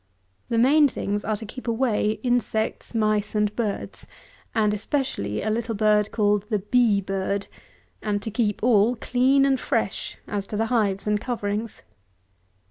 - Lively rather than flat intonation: No, narrow, 2.5 semitones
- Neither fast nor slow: Yes, average, 155 wpm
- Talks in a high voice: Yes, high, 215 Hz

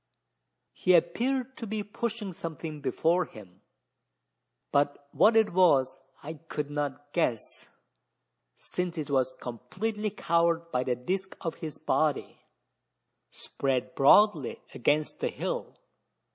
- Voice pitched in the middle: Yes, medium, 160 Hz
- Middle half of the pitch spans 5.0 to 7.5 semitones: Yes, wide, 5.4 semitones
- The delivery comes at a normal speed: No, slow, 115 wpm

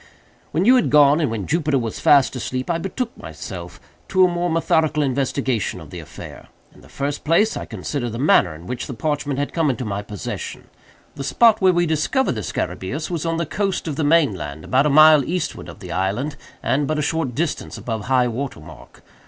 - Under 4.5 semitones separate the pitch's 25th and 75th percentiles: No, average, 5.1 semitones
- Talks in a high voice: No, medium, 145 Hz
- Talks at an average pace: No, fast, 215 wpm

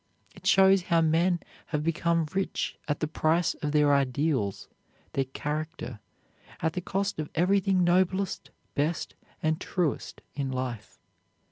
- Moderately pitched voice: Yes, medium, 160 Hz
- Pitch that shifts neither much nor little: Yes, average, 3.4 semitones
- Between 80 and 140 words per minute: Yes, slow, 135 wpm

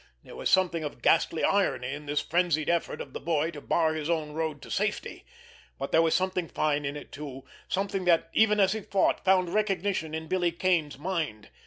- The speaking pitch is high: No, medium, 165 Hz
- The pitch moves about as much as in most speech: Yes, average, 3.8 semitones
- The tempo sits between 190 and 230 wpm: Yes, fast, 205 wpm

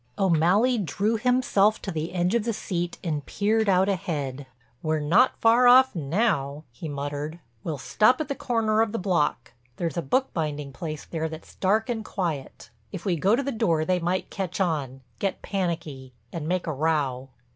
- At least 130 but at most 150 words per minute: No, average, 180 wpm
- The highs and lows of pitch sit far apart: Yes, wide, 5.9 semitones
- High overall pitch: No, medium, 175 Hz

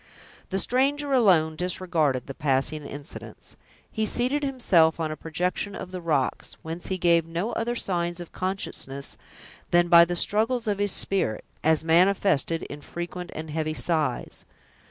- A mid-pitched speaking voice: Yes, medium, 175 Hz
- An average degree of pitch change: Yes, average, 4.0 semitones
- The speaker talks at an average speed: Yes, average, 155 wpm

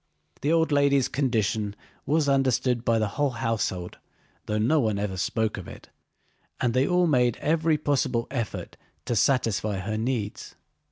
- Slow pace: No, average, 155 wpm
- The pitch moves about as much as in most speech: Yes, average, 4.6 semitones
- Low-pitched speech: Yes, low, 120 Hz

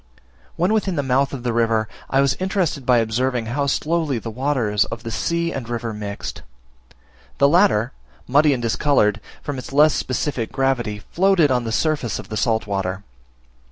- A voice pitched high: No, low, 130 Hz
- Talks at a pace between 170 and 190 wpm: Yes, average, 175 wpm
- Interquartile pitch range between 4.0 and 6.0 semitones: Yes, average, 4.5 semitones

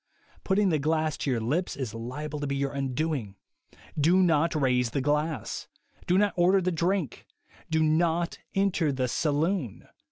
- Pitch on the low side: No, medium, 155 Hz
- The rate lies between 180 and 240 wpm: No, average, 160 wpm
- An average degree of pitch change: Yes, average, 4.0 semitones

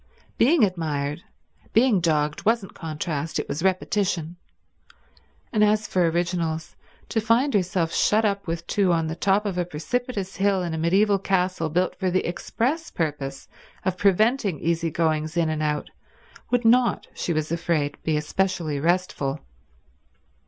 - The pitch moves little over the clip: No, average, 4.2 semitones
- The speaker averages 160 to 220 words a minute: No, average, 150 wpm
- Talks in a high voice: No, medium, 180 Hz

